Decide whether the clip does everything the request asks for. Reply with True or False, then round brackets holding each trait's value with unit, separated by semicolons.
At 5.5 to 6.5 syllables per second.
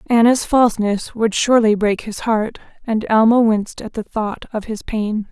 False (4.7 syllables/s)